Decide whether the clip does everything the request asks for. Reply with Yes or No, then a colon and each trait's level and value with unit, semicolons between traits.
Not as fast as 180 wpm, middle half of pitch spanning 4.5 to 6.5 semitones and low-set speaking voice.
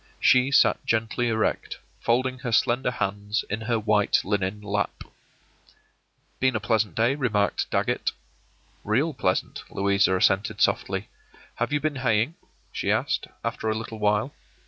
No: average, 140 wpm; average, 3.3 semitones; low, 110 Hz